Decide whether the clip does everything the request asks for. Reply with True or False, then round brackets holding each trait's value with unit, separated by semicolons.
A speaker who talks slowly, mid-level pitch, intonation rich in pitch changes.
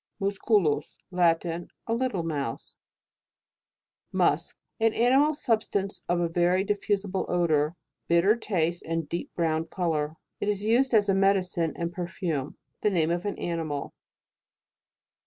False (130 wpm; 175 Hz; 3.7 semitones)